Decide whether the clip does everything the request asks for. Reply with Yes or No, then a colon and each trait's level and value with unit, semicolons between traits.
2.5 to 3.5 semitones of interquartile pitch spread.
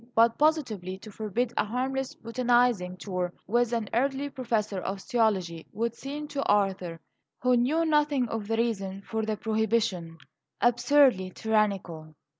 No: average, 4.3 semitones